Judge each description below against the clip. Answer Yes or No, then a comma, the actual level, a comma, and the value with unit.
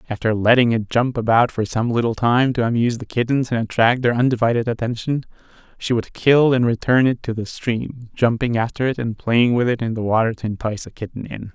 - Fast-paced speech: Yes, fast, 220 wpm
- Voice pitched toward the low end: Yes, low, 120 Hz